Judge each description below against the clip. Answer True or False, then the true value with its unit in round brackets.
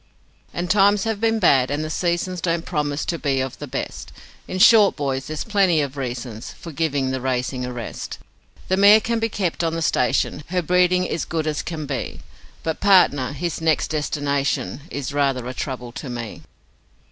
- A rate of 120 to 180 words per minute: False (190 wpm)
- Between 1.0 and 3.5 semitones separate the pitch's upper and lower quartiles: False (5.3 semitones)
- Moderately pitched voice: True (155 Hz)